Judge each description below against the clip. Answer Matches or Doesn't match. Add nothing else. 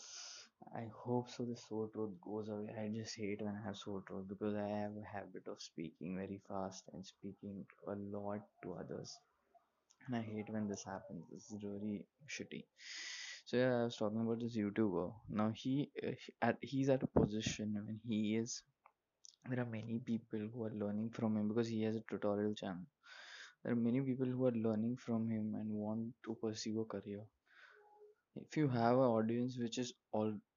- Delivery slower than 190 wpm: Doesn't match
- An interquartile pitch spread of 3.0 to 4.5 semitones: Doesn't match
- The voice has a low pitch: Matches